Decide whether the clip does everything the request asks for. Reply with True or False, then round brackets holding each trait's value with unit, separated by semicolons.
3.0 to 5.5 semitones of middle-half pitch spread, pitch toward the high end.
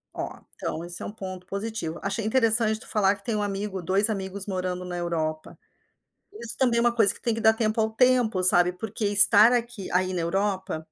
True (3.3 semitones; 200 Hz)